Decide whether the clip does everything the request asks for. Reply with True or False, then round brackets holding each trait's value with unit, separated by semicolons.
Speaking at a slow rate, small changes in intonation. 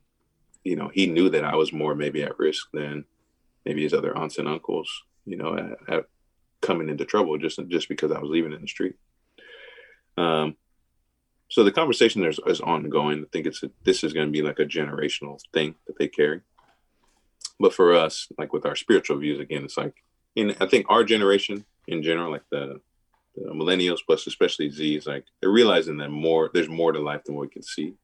False (205 wpm; 2.0 semitones)